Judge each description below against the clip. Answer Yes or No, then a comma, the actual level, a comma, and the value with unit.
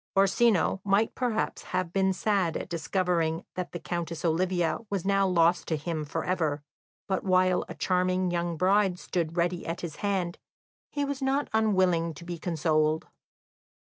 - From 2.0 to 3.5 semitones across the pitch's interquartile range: Yes, narrow, 2.6 semitones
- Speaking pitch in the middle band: Yes, medium, 180 Hz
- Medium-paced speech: Yes, average, 160 wpm